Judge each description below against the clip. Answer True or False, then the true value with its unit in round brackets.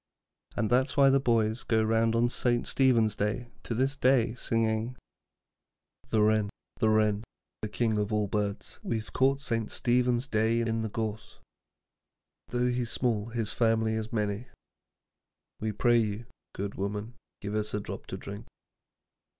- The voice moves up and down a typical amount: False (2.2 semitones)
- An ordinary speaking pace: True (155 wpm)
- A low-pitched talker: True (115 Hz)